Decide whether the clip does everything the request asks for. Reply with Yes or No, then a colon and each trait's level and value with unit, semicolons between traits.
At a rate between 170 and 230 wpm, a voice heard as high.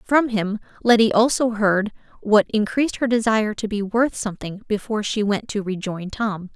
Yes: average, 175 wpm; high, 215 Hz